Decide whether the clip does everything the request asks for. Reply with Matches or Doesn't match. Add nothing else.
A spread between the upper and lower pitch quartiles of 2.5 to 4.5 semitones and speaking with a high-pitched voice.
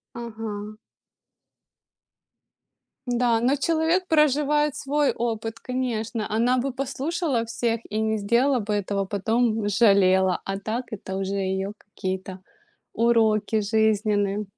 Matches